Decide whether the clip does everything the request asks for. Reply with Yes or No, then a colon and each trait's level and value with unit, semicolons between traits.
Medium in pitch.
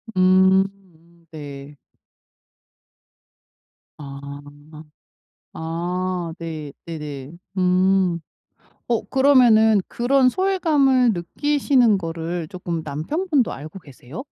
Yes: medium, 180 Hz